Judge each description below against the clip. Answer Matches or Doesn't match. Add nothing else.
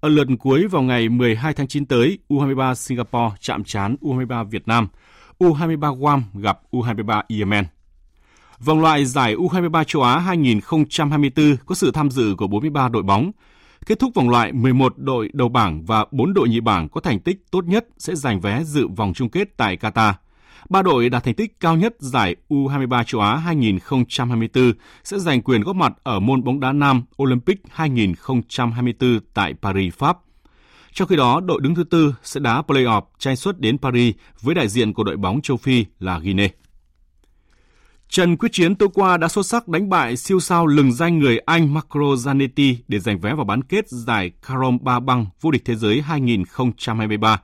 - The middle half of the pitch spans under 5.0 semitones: Doesn't match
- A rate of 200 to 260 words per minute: Doesn't match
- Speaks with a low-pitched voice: Matches